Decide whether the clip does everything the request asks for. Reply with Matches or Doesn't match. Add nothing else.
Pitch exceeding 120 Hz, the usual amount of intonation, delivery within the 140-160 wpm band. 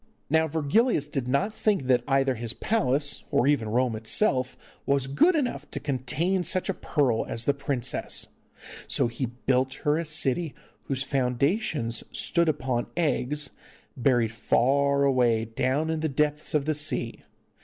Matches